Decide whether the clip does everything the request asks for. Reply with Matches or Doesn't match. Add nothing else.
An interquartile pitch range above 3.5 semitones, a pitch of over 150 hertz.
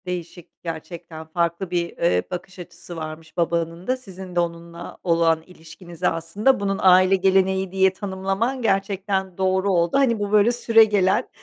Doesn't match